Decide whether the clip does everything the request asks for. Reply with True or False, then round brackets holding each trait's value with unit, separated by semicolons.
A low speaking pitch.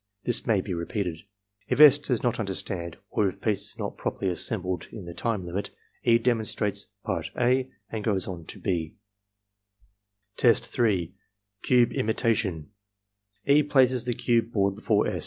True (105 Hz)